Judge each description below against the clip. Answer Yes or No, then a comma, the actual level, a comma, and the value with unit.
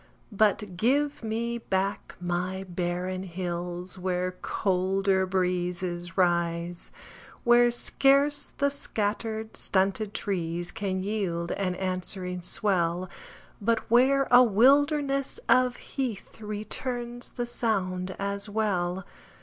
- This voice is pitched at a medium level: No, high, 195 Hz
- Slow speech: Yes, slow, 100 wpm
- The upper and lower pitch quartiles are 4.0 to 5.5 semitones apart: Yes, average, 4.3 semitones